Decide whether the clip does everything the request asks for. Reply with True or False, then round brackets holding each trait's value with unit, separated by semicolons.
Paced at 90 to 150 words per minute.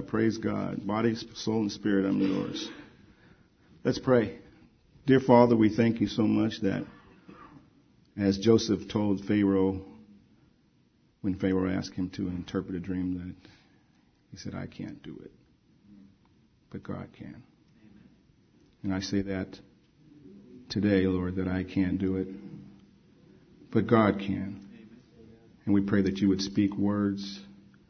True (135 wpm)